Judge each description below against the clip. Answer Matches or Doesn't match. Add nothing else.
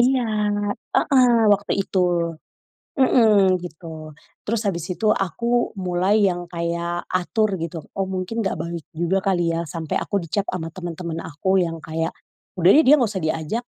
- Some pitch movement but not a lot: Matches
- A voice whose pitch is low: Doesn't match